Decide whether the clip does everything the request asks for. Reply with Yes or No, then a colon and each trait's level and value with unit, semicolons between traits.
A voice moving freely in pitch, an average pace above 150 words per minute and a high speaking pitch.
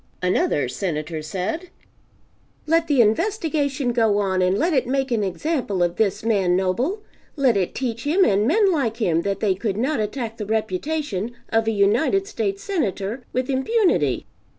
Yes: wide, 6.9 semitones; average, 165 wpm; high, 225 Hz